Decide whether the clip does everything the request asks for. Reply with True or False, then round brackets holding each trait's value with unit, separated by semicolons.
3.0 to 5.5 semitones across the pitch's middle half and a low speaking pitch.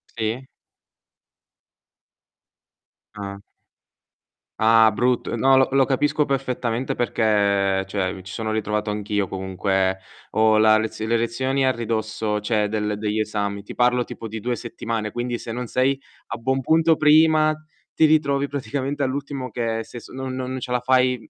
True (3.7 semitones; 115 Hz)